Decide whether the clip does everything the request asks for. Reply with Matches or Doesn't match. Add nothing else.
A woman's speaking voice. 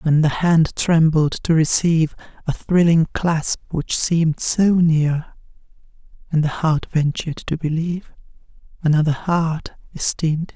Matches